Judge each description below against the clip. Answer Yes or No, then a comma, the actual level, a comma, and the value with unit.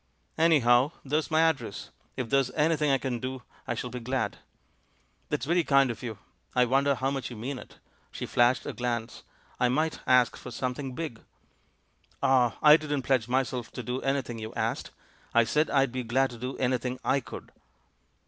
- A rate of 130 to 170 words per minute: No, average, 185 wpm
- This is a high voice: No, low, 130 Hz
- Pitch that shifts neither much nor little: No, narrow, 2.3 semitones